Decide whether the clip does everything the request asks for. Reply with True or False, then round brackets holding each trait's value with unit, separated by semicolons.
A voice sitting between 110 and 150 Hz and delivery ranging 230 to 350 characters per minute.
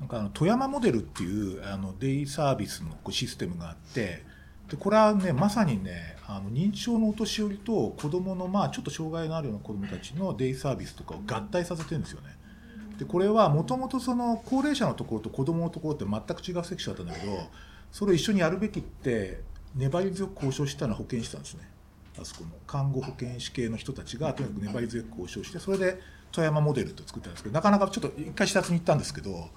False (140 Hz; 470 characters per minute)